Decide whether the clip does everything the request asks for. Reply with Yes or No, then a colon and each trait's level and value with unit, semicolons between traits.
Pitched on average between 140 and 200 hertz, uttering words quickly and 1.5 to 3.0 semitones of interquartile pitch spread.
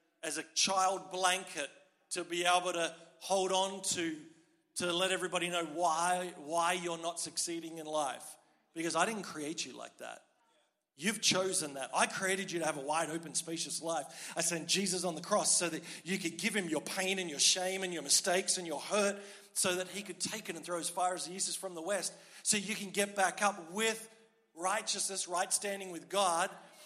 Yes: medium, 185 Hz; fast, 210 wpm; average, 2.7 semitones